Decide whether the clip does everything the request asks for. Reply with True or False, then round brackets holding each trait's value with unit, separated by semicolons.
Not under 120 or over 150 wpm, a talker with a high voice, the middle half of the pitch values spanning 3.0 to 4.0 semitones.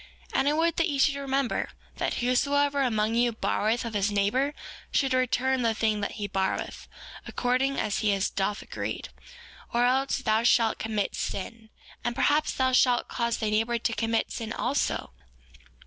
False (170 wpm; 240 Hz; 3.6 semitones)